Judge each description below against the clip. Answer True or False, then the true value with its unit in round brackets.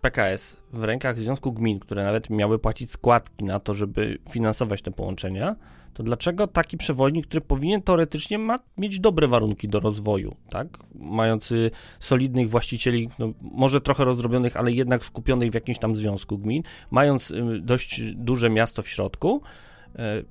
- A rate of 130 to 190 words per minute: True (155 wpm)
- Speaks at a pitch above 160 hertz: False (120 Hz)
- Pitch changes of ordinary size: True (3.7 semitones)